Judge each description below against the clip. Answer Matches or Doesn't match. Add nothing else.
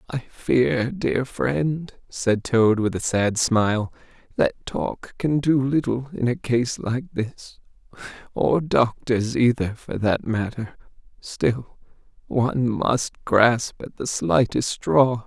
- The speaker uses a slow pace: Matches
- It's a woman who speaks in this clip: Doesn't match